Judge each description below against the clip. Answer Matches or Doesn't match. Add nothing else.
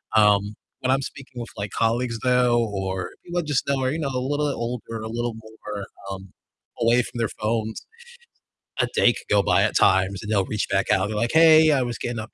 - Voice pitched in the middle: Doesn't match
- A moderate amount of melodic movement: Matches